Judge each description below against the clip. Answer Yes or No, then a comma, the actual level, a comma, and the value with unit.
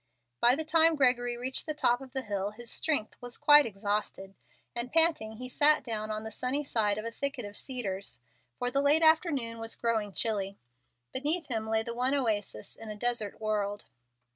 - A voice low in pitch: No, high, 240 Hz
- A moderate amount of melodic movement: Yes, average, 4.5 semitones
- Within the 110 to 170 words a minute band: No, average, 190 wpm